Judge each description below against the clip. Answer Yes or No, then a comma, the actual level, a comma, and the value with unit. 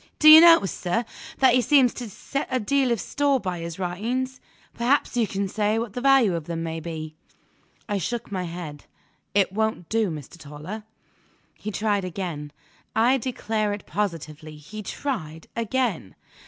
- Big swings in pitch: Yes, wide, 6.3 semitones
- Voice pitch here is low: No, high, 210 Hz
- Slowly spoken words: No, average, 165 wpm